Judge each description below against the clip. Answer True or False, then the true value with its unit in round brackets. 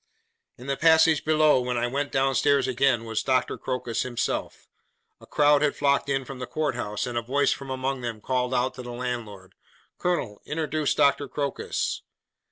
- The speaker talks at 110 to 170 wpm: False (180 wpm)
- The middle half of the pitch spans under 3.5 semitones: True (2.8 semitones)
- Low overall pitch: True (130 Hz)